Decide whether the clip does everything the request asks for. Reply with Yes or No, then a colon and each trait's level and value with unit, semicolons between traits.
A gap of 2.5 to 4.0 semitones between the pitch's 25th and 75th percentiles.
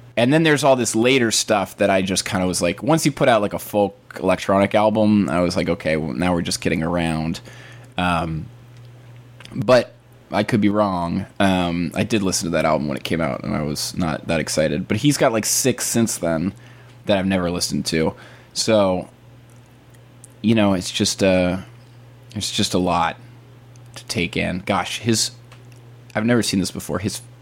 No: average, 5.0 semitones